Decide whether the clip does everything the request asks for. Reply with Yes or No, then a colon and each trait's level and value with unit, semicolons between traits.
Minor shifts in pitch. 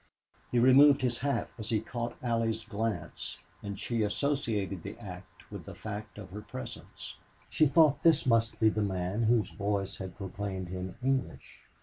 No: average, 3.6 semitones